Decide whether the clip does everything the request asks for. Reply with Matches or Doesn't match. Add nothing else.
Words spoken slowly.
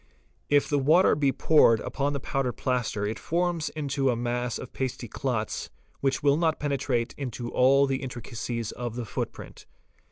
Doesn't match